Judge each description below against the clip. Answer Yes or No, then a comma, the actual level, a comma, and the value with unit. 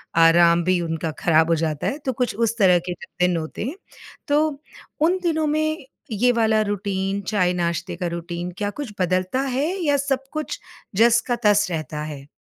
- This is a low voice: No, high, 200 Hz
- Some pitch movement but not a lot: No, wide, 7.2 semitones